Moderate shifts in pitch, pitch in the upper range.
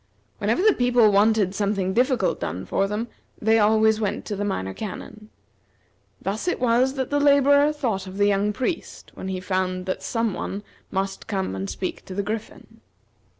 Yes: average, 3.8 semitones; high, 210 Hz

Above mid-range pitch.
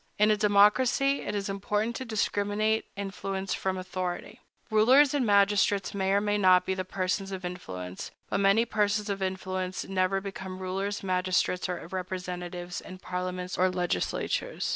Yes: high, 195 Hz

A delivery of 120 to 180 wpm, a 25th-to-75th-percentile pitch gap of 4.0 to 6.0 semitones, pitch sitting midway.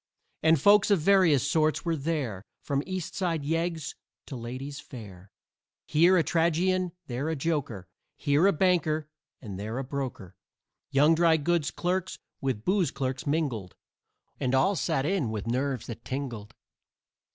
Yes: average, 150 wpm; average, 4.8 semitones; medium, 145 Hz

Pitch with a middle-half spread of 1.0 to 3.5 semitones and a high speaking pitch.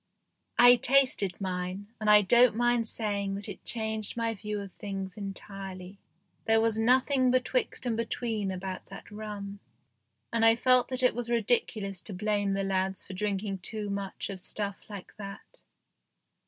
Yes: average, 2.8 semitones; high, 210 Hz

